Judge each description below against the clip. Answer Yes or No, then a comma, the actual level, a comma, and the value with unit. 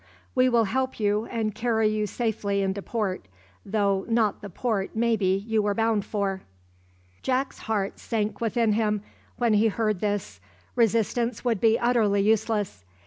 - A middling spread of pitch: No, narrow, 2.2 semitones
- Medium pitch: No, high, 215 Hz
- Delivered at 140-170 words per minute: Yes, average, 150 wpm